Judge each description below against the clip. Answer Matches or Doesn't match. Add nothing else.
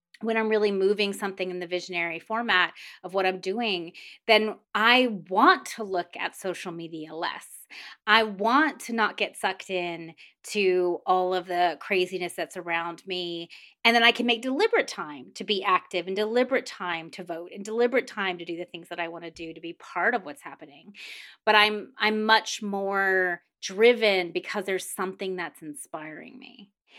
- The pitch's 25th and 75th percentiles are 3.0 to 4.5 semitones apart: Matches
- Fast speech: Doesn't match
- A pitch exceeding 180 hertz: Matches